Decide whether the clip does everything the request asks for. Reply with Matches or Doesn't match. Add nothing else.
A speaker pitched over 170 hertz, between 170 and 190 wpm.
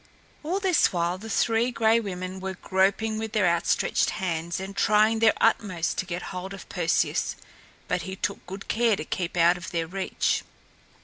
Matches